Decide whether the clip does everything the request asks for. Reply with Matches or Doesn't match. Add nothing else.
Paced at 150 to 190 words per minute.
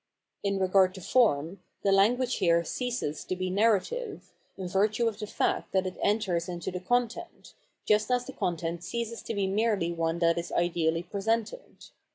Matches